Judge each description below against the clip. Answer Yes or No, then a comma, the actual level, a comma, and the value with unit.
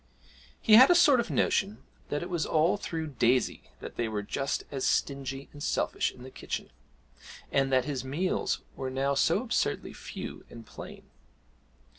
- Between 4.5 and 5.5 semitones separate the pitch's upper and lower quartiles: Yes, average, 4.9 semitones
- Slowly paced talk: No, average, 170 wpm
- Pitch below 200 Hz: Yes, medium, 140 Hz